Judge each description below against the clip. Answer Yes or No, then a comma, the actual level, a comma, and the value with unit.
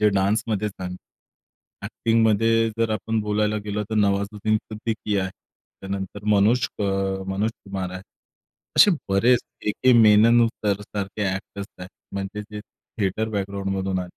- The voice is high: No, low, 105 Hz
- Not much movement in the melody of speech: Yes, narrow, 2.0 semitones